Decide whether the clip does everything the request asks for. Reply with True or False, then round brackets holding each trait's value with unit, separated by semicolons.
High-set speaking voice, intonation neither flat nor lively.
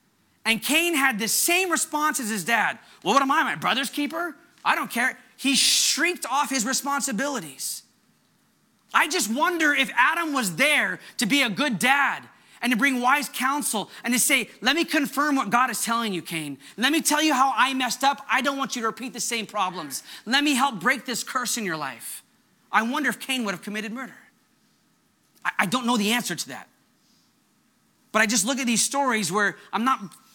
True (255 Hz; 3.8 semitones)